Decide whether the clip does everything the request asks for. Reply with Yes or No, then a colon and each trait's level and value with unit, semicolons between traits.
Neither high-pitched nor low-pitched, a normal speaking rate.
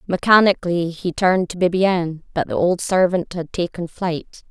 Yes: medium, 180 Hz; average, 160 wpm